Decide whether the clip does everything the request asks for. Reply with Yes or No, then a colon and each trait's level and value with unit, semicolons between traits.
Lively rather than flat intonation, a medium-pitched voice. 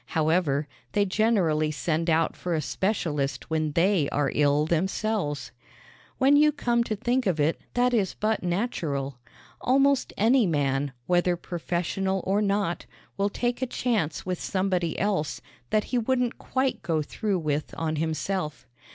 Yes: wide, 5.8 semitones; medium, 180 Hz